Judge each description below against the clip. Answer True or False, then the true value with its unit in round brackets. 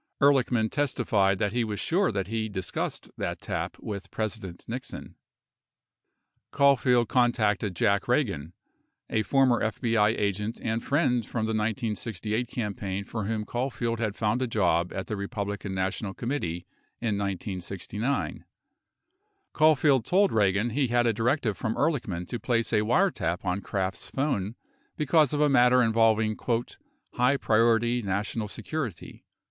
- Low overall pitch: True (110 Hz)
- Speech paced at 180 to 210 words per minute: False (140 wpm)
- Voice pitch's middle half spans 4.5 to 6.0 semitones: False (3.6 semitones)